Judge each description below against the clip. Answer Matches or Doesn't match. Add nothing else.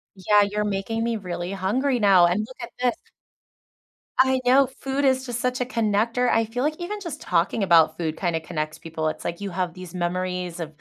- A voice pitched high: Matches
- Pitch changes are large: Matches